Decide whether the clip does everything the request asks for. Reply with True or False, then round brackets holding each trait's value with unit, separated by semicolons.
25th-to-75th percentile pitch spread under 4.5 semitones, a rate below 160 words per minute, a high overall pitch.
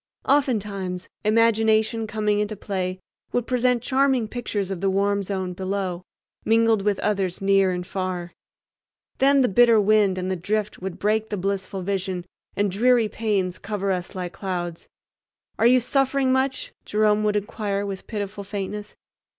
True (2.7 semitones; 150 wpm; 205 Hz)